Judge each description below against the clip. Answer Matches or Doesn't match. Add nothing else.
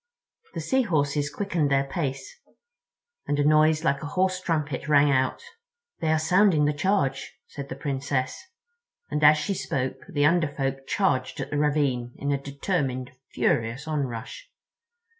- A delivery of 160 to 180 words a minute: Doesn't match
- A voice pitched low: Doesn't match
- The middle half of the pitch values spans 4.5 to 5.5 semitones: Doesn't match